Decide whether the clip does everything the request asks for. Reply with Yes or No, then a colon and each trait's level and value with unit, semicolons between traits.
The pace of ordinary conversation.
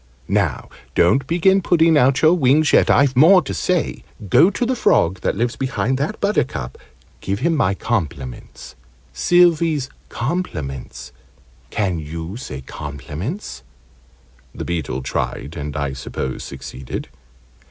No: slow, 130 wpm